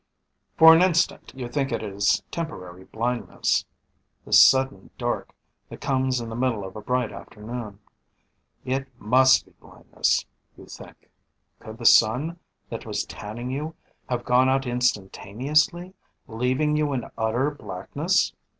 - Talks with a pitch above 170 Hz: No, low, 125 Hz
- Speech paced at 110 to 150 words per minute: Yes, average, 140 wpm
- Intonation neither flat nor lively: Yes, average, 4.2 semitones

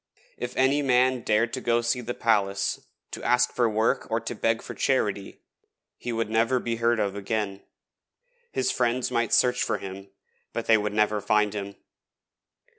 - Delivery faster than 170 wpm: Yes, average, 180 wpm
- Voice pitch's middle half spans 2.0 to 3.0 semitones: Yes, average, 2.7 semitones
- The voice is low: Yes, low, 115 Hz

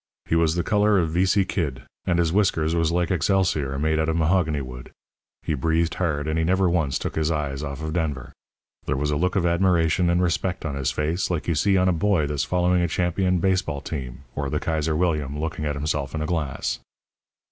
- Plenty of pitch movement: No, average, 3.2 semitones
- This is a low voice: Yes, very low, 80 Hz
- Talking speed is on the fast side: Yes, fast, 225 wpm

